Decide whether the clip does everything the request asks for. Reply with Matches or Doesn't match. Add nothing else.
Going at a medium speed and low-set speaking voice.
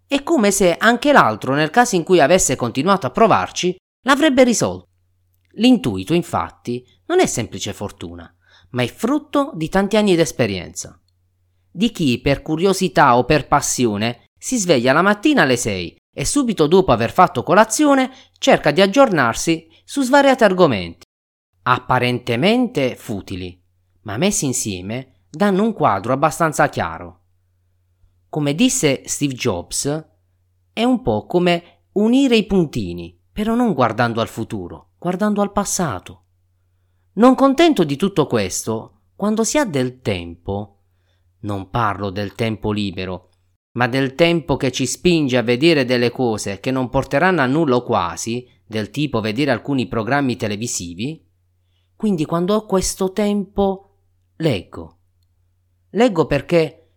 Matches